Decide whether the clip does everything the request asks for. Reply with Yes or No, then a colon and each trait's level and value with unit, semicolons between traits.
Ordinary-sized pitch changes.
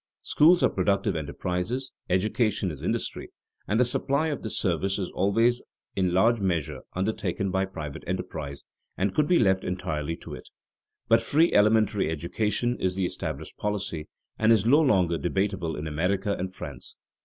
Yes: average, 3.8 semitones